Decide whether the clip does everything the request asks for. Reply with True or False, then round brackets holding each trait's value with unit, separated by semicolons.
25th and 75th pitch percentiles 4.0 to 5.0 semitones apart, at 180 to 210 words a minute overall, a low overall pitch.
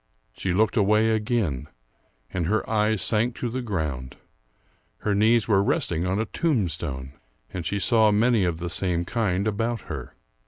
False (4.3 semitones; 160 wpm; 105 Hz)